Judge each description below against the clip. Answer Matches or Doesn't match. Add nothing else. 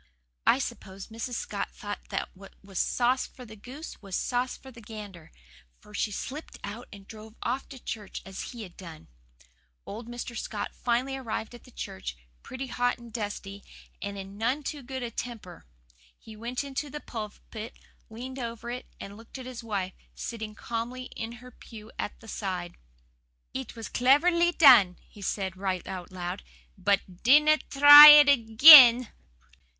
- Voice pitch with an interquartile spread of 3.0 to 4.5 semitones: Matches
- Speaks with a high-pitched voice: Matches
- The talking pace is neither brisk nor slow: Matches